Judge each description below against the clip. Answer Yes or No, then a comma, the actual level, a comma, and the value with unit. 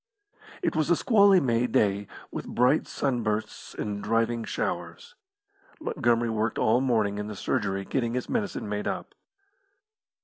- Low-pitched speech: Yes, low, 115 Hz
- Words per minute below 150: Yes, average, 140 wpm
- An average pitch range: Yes, average, 4.4 semitones